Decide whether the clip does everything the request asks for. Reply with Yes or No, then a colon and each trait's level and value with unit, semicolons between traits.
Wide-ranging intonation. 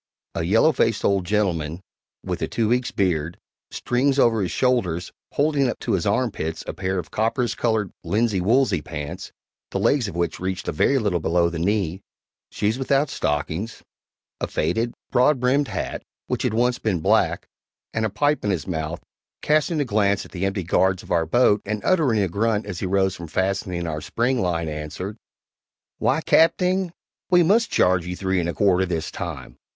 Yes: wide, 5.7 semitones